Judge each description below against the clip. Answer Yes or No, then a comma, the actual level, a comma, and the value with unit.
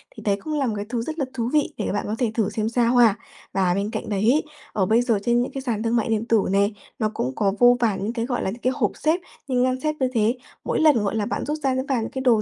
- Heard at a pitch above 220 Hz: Yes, high, 230 Hz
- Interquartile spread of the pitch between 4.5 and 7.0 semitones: No, average, 3.2 semitones